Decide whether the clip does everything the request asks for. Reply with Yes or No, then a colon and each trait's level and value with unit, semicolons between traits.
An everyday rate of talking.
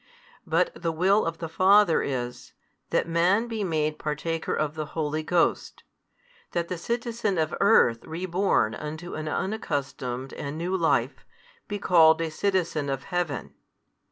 Yes: average, 145 wpm